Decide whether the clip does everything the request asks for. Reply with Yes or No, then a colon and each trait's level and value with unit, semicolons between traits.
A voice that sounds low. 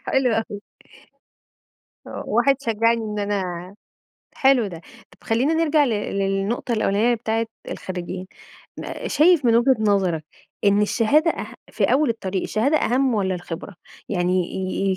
No: high, 215 Hz